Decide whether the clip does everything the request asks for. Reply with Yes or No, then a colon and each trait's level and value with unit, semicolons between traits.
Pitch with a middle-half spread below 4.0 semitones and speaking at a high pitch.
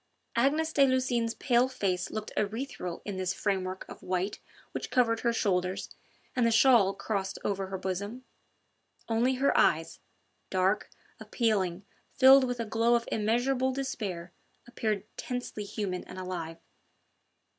No: average, 4.6 semitones; high, 220 Hz